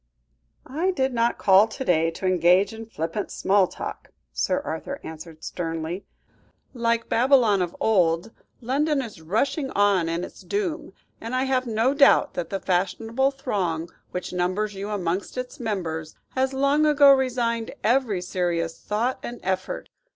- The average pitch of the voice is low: No, high, 215 Hz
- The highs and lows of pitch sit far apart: Yes, wide, 6.5 semitones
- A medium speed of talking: Yes, average, 150 wpm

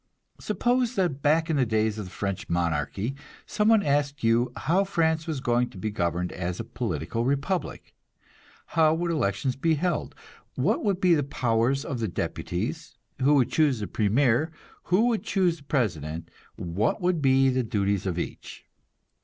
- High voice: No, low, 135 Hz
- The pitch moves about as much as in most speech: No, wide, 7.4 semitones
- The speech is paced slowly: No, average, 170 wpm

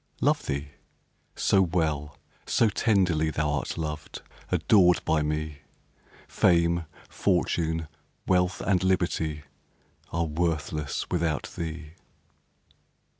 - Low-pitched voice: Yes, very low, 80 Hz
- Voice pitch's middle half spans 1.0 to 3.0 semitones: Yes, average, 2.7 semitones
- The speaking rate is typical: No, slow, 90 wpm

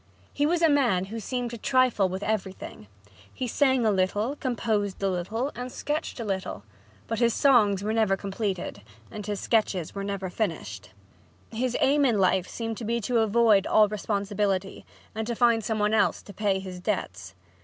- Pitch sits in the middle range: No, high, 215 Hz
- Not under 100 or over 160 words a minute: No, average, 180 wpm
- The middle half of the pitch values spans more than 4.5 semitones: No, average, 3.4 semitones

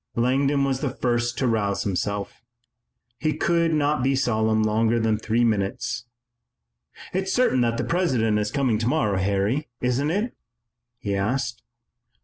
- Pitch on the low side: Yes, low, 120 Hz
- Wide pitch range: No, average, 4.3 semitones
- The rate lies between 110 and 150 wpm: Yes, average, 140 wpm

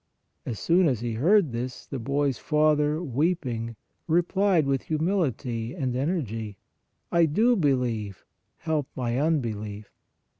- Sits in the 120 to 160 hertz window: Yes, medium, 140 Hz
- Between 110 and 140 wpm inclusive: Yes, slow, 135 wpm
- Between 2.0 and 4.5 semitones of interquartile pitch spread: No, wide, 5.6 semitones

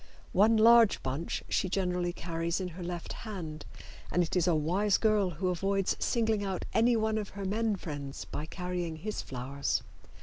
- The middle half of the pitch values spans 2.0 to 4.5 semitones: Yes, average, 4.1 semitones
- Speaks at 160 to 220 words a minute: Yes, average, 170 wpm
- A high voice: No, medium, 180 Hz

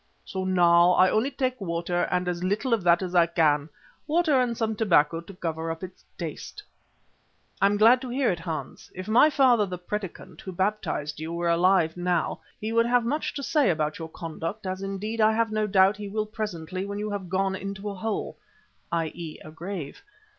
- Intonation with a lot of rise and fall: No, average, 4.1 semitones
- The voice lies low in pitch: No, high, 190 Hz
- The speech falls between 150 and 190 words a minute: No, fast, 205 wpm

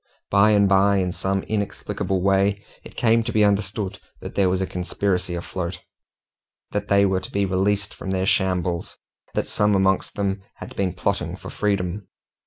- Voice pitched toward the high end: No, very low, 95 Hz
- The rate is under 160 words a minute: No, average, 175 wpm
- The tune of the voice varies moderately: No, narrow, 1.4 semitones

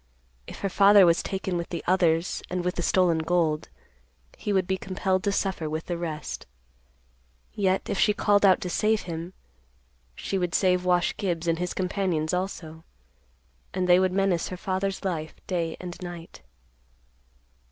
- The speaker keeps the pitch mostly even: Yes, narrow, 2.1 semitones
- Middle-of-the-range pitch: Yes, medium, 180 Hz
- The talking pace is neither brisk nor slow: Yes, average, 165 wpm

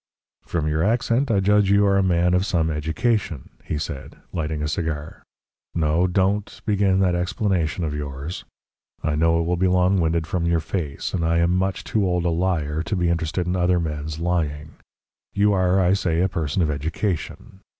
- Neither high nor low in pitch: No, very low, 85 Hz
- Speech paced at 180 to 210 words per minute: Yes, average, 190 wpm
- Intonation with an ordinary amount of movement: Yes, average, 3.1 semitones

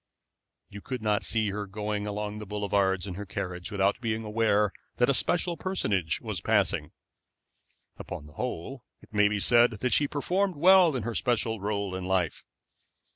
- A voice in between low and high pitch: No, low, 105 Hz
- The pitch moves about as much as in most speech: Yes, average, 3.5 semitones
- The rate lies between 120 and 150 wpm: No, average, 170 wpm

